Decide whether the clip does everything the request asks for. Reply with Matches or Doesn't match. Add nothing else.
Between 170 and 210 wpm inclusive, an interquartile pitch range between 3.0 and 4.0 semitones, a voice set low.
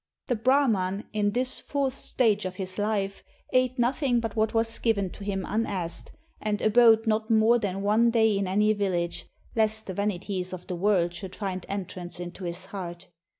Doesn't match